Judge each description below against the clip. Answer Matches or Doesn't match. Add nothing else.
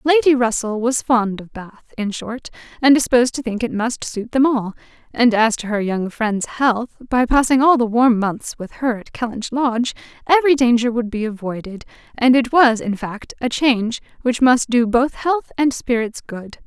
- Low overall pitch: Doesn't match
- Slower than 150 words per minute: Doesn't match